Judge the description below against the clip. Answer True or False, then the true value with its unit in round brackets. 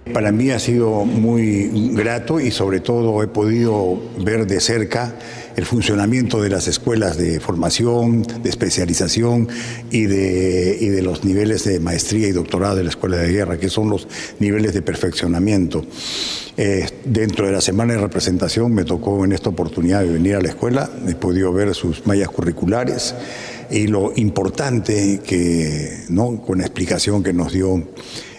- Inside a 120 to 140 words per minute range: False (165 wpm)